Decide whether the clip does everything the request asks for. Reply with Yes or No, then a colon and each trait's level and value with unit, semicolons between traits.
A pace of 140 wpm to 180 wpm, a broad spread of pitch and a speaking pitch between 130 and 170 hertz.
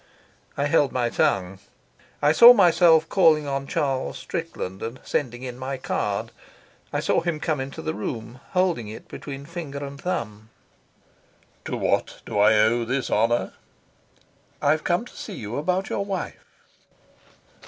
Yes: average, 150 wpm; wide, 5.8 semitones; medium, 140 Hz